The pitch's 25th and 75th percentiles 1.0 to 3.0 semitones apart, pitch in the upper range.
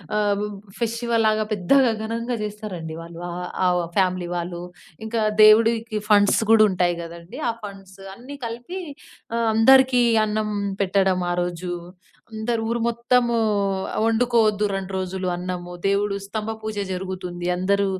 No: average, 3.8 semitones; high, 210 Hz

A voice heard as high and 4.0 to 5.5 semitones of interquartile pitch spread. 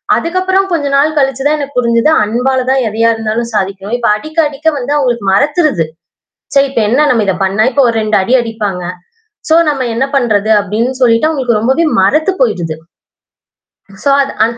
Yes: high, 245 Hz; average, 4.6 semitones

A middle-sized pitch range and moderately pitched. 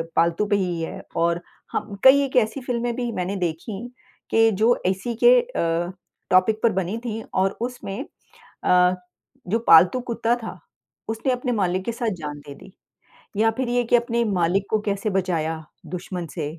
No: average, 4.7 semitones; high, 205 Hz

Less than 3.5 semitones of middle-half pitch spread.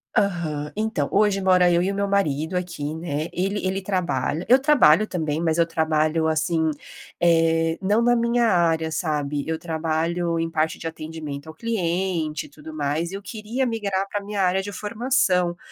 No: average, 3.8 semitones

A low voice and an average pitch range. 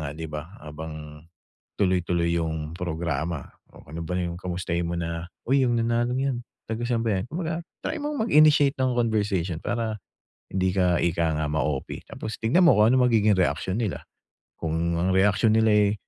No: very low, 95 Hz; wide, 5.8 semitones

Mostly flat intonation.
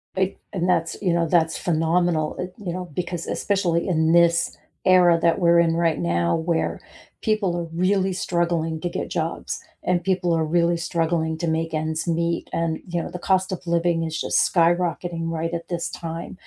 Yes: narrow, 1.4 semitones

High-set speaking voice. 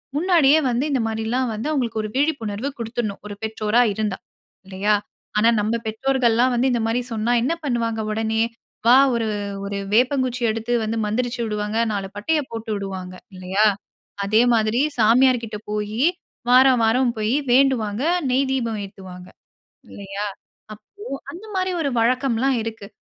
Yes: high, 230 Hz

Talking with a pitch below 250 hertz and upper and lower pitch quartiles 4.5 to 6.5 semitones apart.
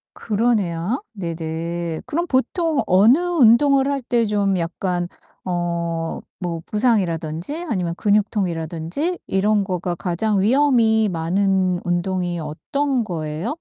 Yes: high, 190 Hz; wide, 5.5 semitones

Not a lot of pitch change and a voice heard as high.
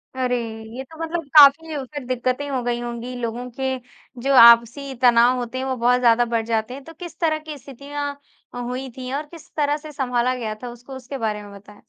No: average, 3.0 semitones; very high, 255 Hz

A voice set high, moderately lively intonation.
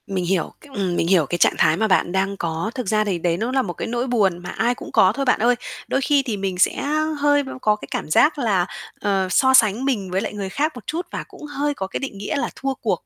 No: high, 215 Hz; wide, 5.9 semitones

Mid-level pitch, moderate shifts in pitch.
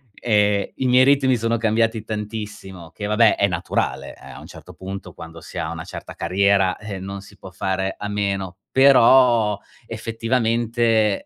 No: low, 105 Hz; average, 3.0 semitones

